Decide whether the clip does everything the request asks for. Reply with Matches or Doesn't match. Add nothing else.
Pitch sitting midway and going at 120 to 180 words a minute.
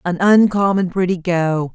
Matches